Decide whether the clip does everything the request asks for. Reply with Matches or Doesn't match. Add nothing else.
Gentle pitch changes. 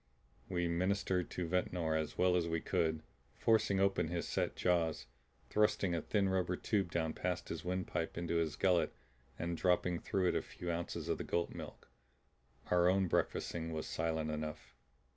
Matches